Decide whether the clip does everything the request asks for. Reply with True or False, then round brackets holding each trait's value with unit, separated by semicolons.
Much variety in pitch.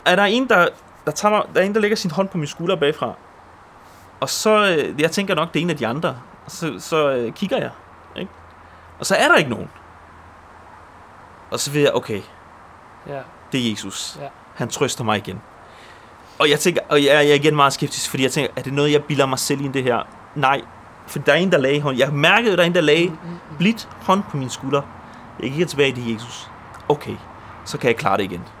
True (6.6 semitones)